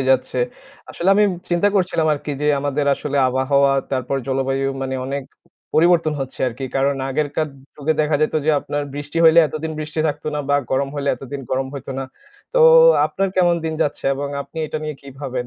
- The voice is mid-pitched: Yes, medium, 145 Hz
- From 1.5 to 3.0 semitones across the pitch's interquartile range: Yes, average, 2.7 semitones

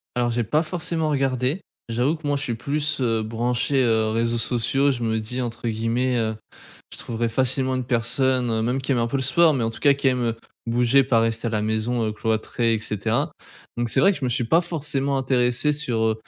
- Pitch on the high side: No, low, 125 Hz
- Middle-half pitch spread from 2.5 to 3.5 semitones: Yes, average, 3.1 semitones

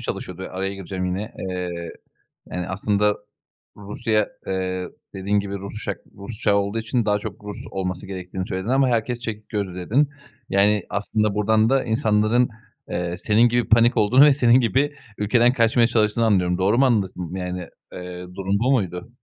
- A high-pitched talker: No, low, 105 Hz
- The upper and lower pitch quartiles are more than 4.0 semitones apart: No, average, 3.6 semitones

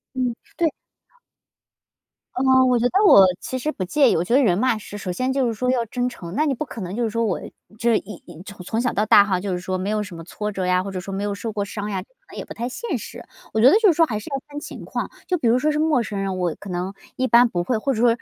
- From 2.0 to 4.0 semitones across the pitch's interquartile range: No, average, 4.9 semitones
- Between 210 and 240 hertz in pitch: Yes, high, 225 Hz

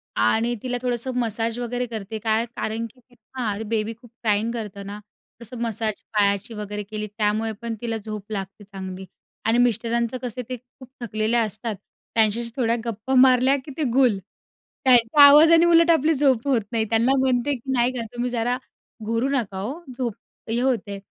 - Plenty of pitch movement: No, narrow, 2.6 semitones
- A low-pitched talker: No, high, 230 Hz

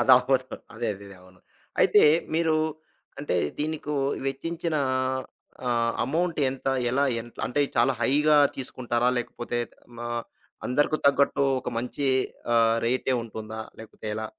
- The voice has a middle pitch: No, low, 130 Hz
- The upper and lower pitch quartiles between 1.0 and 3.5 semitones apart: No, average, 3.9 semitones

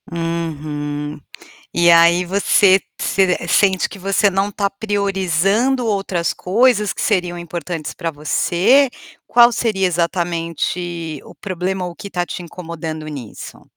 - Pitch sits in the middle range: Yes, medium, 180 Hz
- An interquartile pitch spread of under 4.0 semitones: Yes, average, 2.8 semitones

